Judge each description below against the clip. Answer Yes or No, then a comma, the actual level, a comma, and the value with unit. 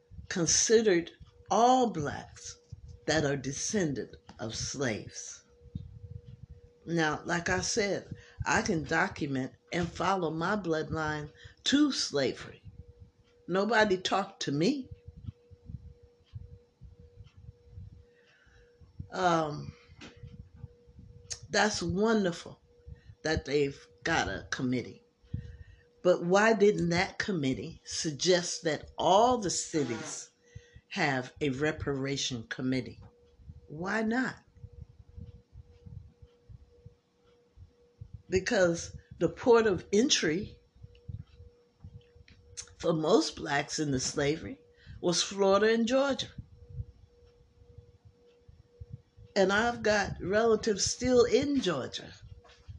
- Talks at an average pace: No, slow, 80 wpm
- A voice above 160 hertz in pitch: No, low, 135 Hz